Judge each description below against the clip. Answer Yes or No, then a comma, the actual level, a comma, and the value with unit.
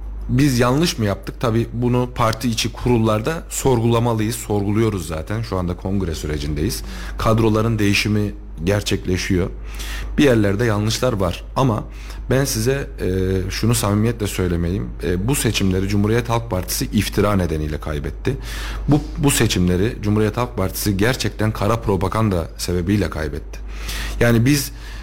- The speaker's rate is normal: Yes, average, 120 wpm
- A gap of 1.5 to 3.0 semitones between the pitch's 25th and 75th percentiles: No, average, 3.9 semitones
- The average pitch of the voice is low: Yes, low, 105 Hz